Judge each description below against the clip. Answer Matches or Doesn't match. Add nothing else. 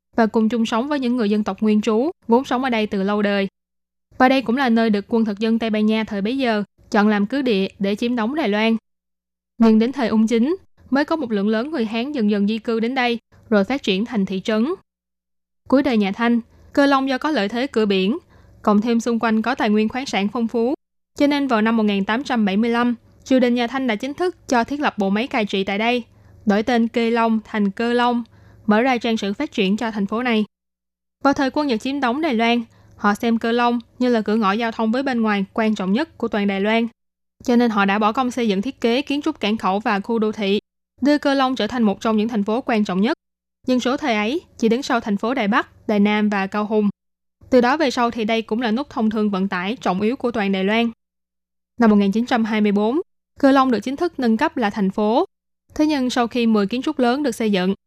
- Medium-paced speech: Doesn't match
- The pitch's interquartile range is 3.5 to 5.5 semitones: Doesn't match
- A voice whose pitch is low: Doesn't match